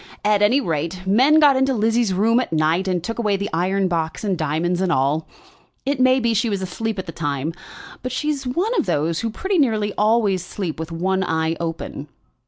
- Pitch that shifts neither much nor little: No, wide, 5.8 semitones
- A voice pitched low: No, high, 195 Hz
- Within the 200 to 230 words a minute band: Yes, fast, 205 wpm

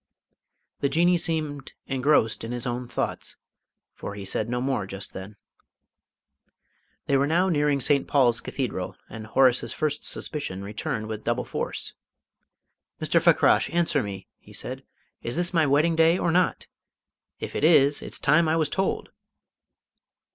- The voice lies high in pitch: No, medium, 140 Hz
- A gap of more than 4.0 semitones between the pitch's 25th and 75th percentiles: Yes, wide, 5.4 semitones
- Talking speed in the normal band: Yes, average, 150 wpm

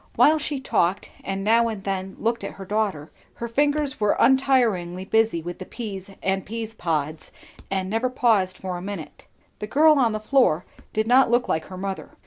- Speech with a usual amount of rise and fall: Yes, average, 4.2 semitones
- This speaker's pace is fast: No, average, 190 wpm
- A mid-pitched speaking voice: No, high, 210 Hz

